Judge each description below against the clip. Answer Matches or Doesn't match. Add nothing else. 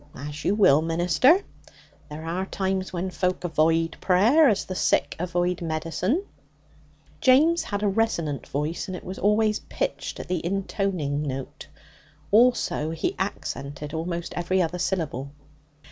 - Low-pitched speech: Doesn't match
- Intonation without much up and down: Doesn't match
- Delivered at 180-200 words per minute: Doesn't match